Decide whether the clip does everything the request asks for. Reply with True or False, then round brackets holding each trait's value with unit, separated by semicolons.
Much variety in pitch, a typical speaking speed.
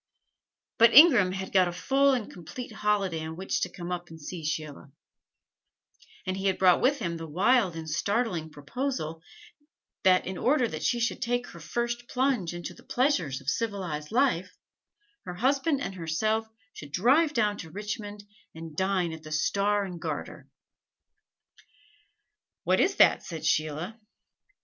True (6.4 semitones; 160 wpm)